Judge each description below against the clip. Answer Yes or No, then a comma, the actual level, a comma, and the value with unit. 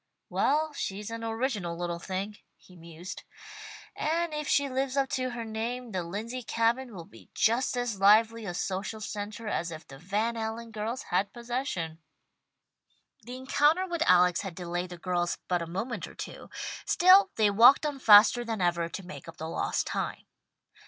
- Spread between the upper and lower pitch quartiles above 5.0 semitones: Yes, wide, 5.6 semitones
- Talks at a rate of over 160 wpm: Yes, average, 175 wpm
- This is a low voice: No, high, 220 Hz